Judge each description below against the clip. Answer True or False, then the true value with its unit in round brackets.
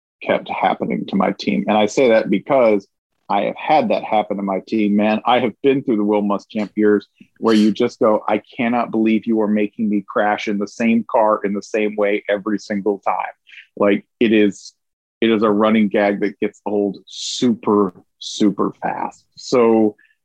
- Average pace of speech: True (195 wpm)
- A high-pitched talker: False (105 Hz)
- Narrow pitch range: True (1.3 semitones)